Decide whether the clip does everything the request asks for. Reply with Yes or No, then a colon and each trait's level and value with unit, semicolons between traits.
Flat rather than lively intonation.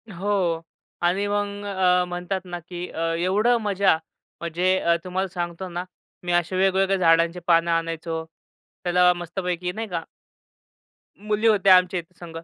Yes: narrow, 2.1 semitones